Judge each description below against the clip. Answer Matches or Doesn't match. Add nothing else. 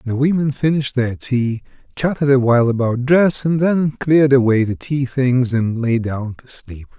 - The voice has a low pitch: Matches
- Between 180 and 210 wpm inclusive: Matches